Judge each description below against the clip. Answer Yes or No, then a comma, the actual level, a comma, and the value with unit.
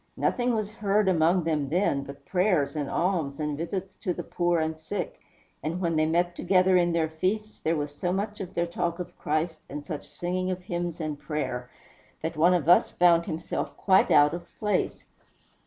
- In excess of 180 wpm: Yes, average, 195 wpm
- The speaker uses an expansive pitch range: No, average, 2.8 semitones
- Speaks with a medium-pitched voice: Yes, medium, 170 Hz